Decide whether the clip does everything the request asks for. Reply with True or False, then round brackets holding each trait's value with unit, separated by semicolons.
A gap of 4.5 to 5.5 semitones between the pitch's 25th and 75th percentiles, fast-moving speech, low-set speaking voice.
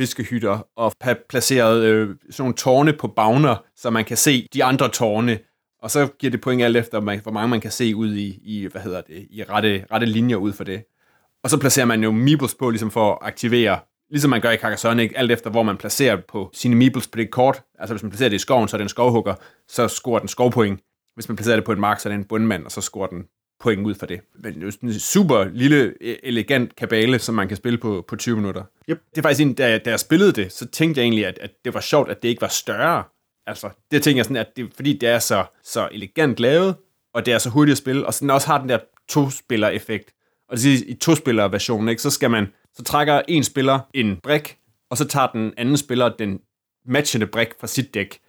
False (3.3 semitones; 245 wpm; 115 Hz)